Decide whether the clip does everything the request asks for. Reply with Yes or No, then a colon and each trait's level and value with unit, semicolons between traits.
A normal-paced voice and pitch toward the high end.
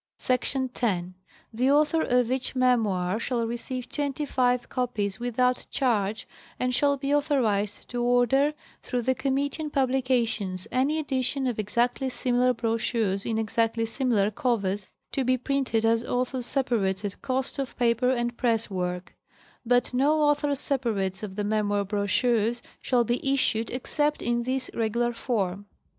Yes: average, 150 wpm; high, 245 Hz